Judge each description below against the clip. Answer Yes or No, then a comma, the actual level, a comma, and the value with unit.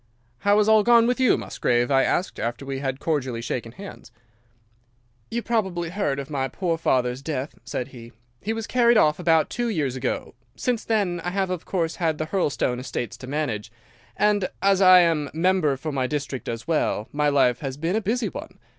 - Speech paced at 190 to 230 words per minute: Yes, average, 200 wpm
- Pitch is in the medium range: Yes, medium, 160 Hz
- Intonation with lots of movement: Yes, wide, 6.7 semitones